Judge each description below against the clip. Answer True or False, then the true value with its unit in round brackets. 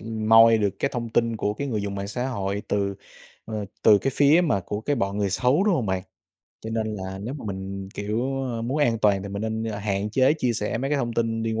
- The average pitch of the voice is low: True (110 Hz)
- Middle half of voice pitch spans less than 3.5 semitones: True (3.1 semitones)